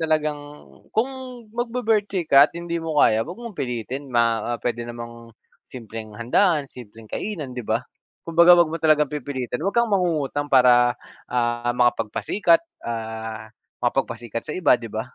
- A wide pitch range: Yes, wide, 6.1 semitones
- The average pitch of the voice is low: Yes, low, 130 Hz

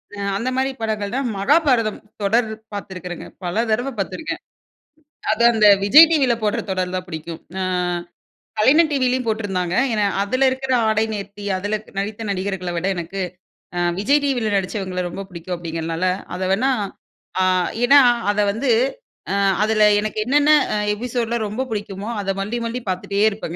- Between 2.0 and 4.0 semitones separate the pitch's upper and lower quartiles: No, average, 4.5 semitones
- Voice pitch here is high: Yes, high, 210 Hz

